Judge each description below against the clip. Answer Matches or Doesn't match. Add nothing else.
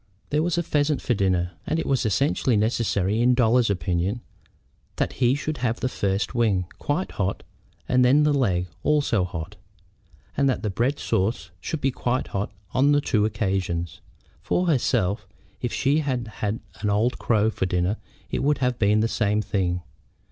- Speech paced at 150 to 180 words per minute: Matches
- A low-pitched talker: Matches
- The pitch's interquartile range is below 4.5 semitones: Doesn't match